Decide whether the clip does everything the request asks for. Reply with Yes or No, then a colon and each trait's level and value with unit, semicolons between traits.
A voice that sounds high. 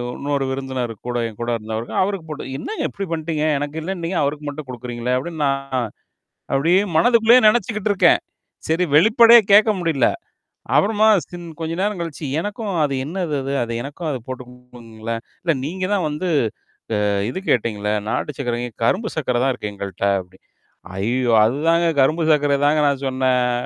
No: medium, 145 Hz